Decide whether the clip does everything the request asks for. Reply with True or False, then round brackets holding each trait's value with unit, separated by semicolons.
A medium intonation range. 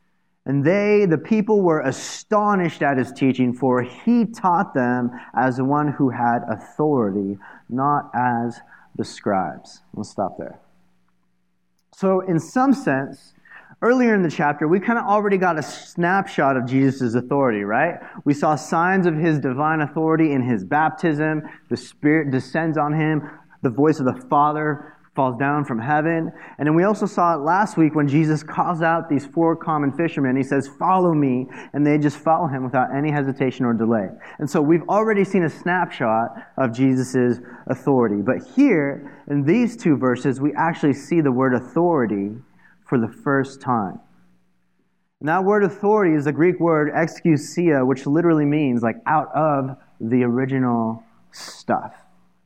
True (4.5 semitones)